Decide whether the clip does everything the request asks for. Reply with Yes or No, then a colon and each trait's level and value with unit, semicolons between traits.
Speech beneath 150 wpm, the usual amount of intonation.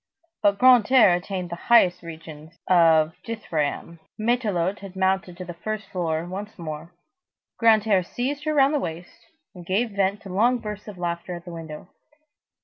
No: average, 165 wpm; average, 4.1 semitones